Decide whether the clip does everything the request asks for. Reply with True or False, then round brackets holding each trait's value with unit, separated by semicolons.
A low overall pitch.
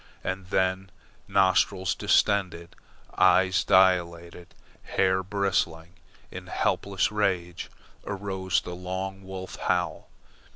True (95 Hz)